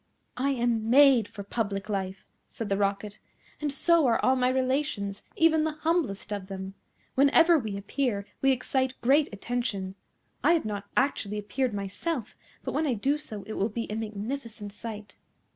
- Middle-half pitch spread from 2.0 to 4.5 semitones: No, average, 5.2 semitones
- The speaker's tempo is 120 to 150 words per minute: No, average, 170 wpm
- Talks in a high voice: Yes, high, 230 Hz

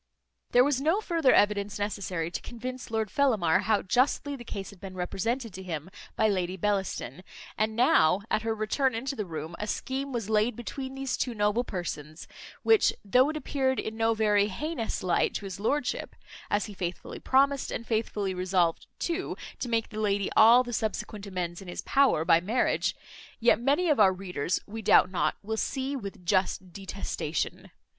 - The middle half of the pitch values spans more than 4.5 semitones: Yes, average, 5.1 semitones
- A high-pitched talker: Yes, high, 215 Hz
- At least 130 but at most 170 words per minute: No, average, 180 wpm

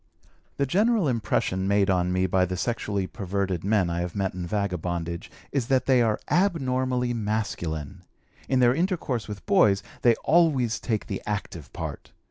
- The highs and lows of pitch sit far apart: Yes, wide, 5.7 semitones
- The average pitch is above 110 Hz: No, low, 105 Hz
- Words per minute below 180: Yes, average, 160 wpm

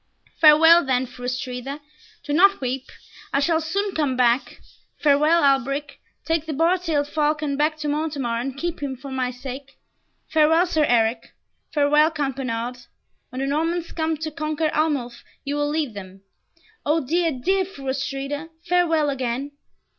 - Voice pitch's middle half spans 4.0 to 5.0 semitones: No, average, 3.3 semitones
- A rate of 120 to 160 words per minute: Yes, average, 155 wpm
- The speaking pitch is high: Yes, very high, 290 Hz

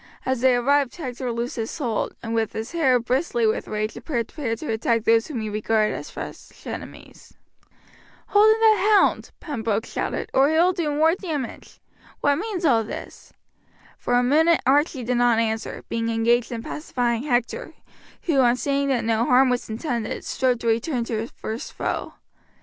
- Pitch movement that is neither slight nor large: Yes, average, 4.4 semitones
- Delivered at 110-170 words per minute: No, average, 180 wpm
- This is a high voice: Yes, high, 245 Hz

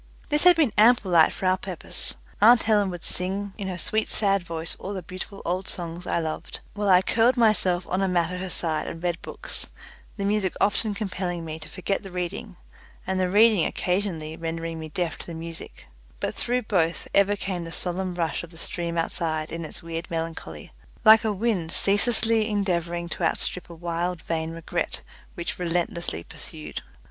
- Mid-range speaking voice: Yes, medium, 180 Hz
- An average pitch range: Yes, average, 3.3 semitones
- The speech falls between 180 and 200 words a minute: Yes, average, 190 wpm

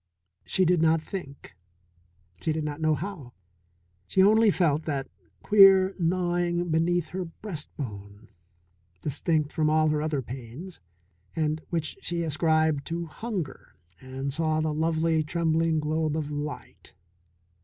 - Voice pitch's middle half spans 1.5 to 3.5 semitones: Yes, narrow, 2.5 semitones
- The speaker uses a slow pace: Yes, slow, 130 wpm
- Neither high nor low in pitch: Yes, medium, 160 Hz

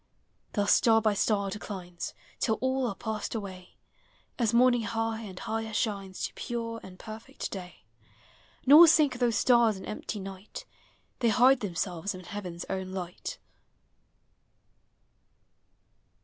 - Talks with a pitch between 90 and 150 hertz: No, high, 215 Hz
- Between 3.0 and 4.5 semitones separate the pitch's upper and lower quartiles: Yes, average, 3.7 semitones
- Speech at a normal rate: No, slow, 130 wpm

